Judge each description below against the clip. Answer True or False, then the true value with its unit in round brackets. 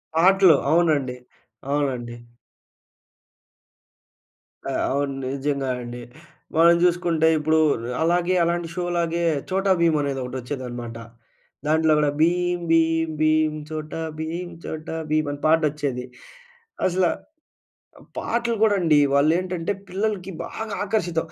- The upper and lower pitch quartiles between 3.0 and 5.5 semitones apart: True (3.4 semitones)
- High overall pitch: False (160 Hz)